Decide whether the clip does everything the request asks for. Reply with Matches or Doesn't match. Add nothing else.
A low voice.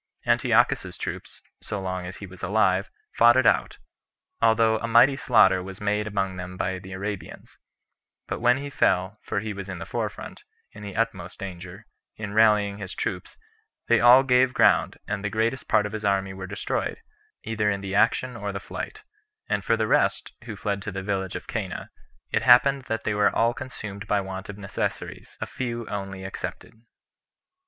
Matches